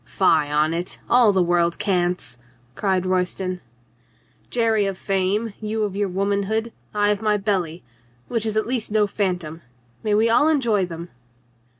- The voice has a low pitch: No, high, 195 Hz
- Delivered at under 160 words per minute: No, average, 165 wpm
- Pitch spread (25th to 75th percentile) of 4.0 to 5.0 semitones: No, average, 3.3 semitones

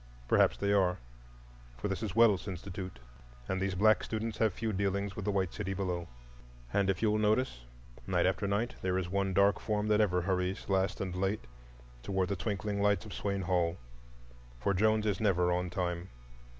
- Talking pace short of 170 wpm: No, average, 185 wpm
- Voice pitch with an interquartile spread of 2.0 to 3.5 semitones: Yes, narrow, 2.4 semitones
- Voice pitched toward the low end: Yes, very low, 95 Hz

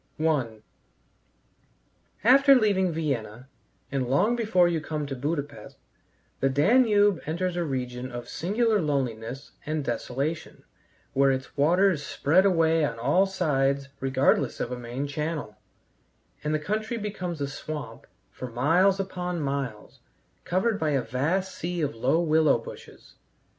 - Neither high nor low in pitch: Yes, medium, 155 Hz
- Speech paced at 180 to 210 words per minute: No, slow, 135 wpm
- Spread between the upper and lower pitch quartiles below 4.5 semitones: No, average, 5.3 semitones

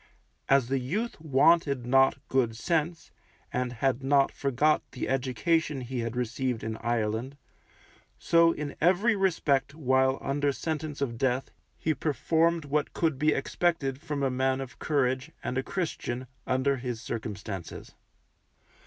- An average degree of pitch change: Yes, average, 3.5 semitones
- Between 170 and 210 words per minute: No, average, 140 wpm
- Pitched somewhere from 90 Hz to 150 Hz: Yes, low, 135 Hz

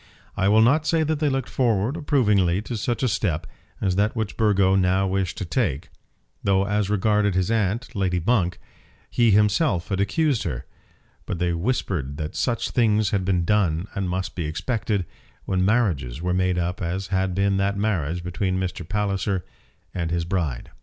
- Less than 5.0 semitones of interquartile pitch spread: Yes, average, 3.3 semitones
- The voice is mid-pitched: No, very low, 95 Hz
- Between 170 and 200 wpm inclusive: Yes, average, 180 wpm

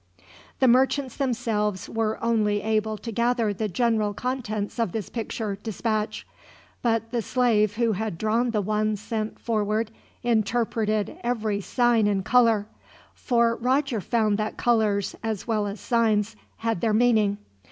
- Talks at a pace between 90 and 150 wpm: Yes, average, 140 wpm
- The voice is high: Yes, high, 220 Hz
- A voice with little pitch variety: Yes, narrow, 2.0 semitones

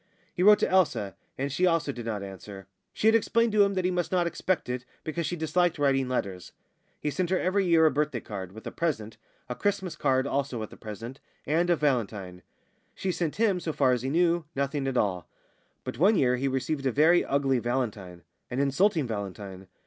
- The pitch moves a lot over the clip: Yes, wide, 7.1 semitones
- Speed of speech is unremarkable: No, fast, 210 wpm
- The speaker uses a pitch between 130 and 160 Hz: Yes, medium, 140 Hz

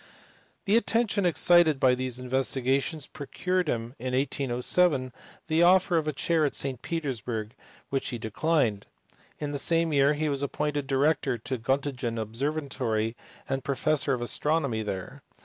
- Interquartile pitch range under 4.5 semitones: Yes, average, 3.9 semitones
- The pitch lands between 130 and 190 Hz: Yes, medium, 140 Hz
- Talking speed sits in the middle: Yes, average, 150 wpm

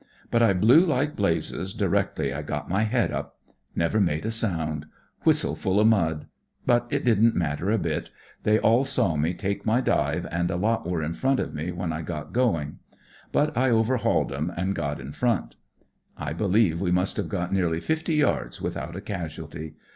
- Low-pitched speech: Yes, very low, 95 Hz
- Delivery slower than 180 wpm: No, average, 190 wpm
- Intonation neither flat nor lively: No, wide, 5.9 semitones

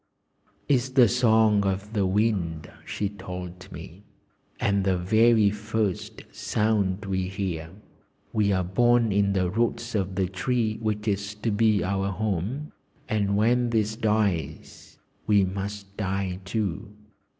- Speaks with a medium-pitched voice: No, low, 100 Hz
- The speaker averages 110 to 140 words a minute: Yes, slow, 135 wpm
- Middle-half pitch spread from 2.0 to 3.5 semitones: Yes, narrow, 2.6 semitones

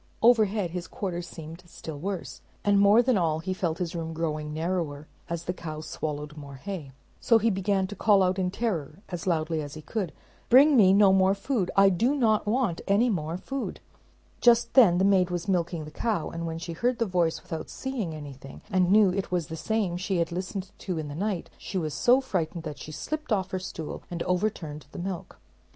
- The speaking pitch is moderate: Yes, medium, 180 Hz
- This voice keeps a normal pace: No, fast, 210 wpm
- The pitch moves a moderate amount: Yes, average, 4.0 semitones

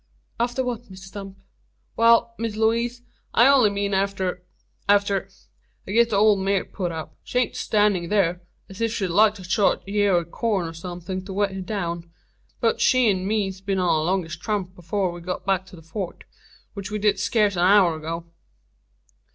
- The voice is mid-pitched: No, high, 195 Hz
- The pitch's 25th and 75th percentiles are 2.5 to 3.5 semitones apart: Yes, average, 2.8 semitones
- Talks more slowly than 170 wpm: No, average, 190 wpm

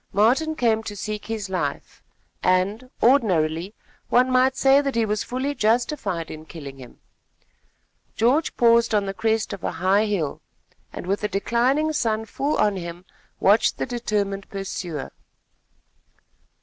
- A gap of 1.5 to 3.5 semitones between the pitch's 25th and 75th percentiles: No, average, 4.3 semitones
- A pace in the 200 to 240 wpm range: No, average, 145 wpm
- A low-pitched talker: No, high, 215 Hz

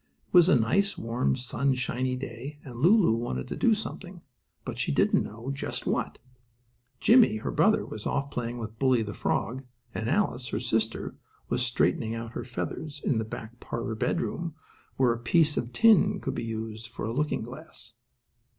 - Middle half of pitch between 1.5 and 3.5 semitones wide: No, average, 4.4 semitones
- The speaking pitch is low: Yes, low, 125 Hz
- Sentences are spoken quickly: No, average, 180 wpm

